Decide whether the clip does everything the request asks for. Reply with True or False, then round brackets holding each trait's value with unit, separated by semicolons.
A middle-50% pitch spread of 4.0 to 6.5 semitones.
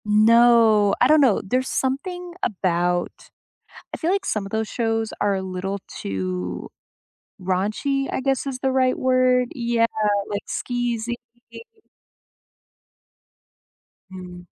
True (5.0 semitones)